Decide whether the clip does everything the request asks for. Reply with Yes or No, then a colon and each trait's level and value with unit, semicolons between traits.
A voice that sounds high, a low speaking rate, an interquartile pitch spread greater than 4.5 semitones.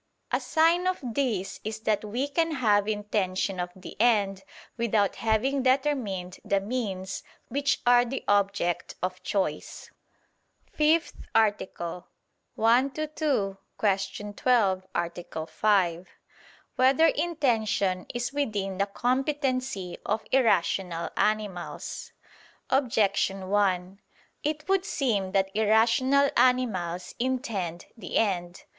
Yes: high, 215 Hz; slow, 110 wpm; average, 5.2 semitones